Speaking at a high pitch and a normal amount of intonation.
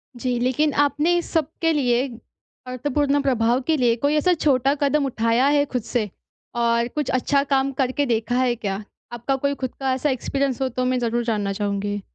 Yes: very high, 255 Hz; average, 3.1 semitones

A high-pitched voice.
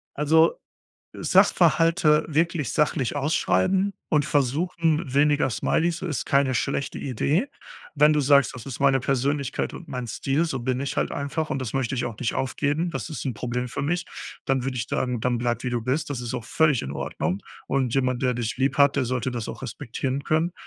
No: low, 135 Hz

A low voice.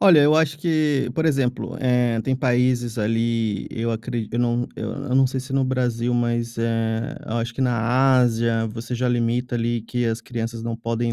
Yes: low, 120 Hz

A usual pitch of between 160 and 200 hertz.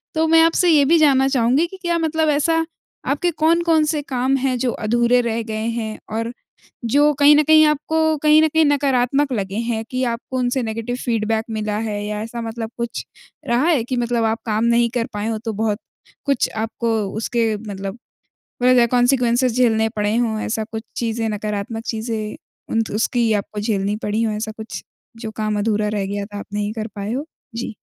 No: high, 235 Hz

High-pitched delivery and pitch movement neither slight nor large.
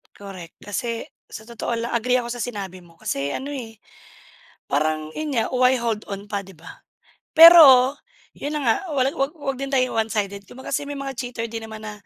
Yes: high, 235 Hz; average, 4.7 semitones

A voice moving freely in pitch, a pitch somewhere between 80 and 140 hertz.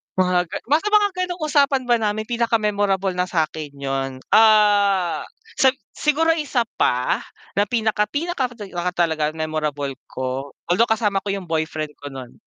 No: wide, 6.9 semitones; high, 200 Hz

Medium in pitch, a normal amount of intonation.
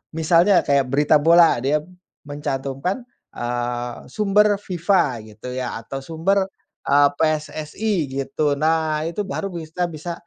Yes: medium, 155 Hz; average, 4.3 semitones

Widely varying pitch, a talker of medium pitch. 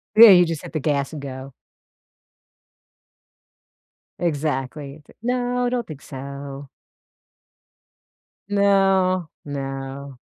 Yes: wide, 5.8 semitones; medium, 150 Hz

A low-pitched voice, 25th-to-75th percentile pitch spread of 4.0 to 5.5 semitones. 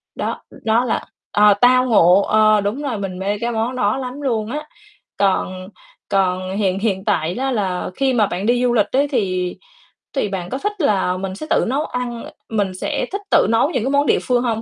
No: high, 215 Hz; average, 4.6 semitones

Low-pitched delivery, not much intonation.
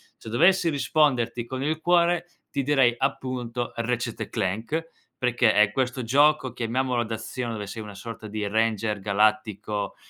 No: low, 120 Hz; average, 3.6 semitones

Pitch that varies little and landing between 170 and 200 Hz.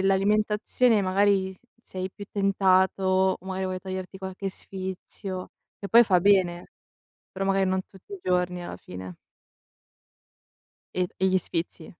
Yes: narrow, 1.0 semitones; high, 190 Hz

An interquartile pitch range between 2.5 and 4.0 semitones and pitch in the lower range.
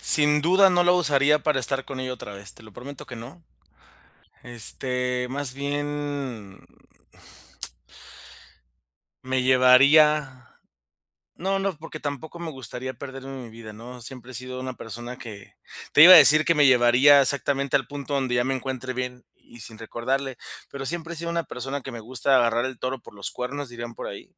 Yes: average, 2.8 semitones; low, 130 Hz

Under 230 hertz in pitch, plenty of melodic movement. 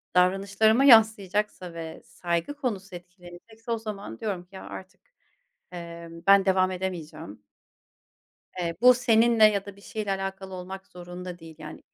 No: high, 190 Hz; average, 3.4 semitones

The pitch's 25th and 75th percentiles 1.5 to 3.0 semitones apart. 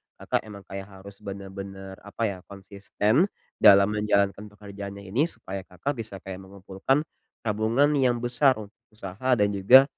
Yes: average, 2.7 semitones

